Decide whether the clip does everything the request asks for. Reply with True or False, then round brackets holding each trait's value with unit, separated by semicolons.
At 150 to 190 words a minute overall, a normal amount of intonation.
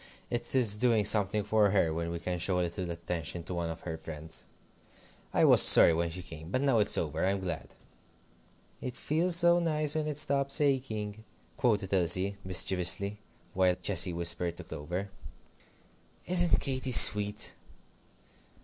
False (160 wpm; 6.4 semitones)